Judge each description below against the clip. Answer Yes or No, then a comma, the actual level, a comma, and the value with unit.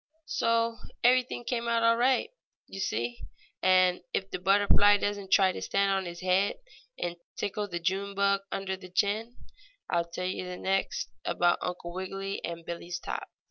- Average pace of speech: Yes, average, 165 wpm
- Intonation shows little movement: Yes, narrow, 2.3 semitones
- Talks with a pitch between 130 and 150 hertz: No, high, 195 Hz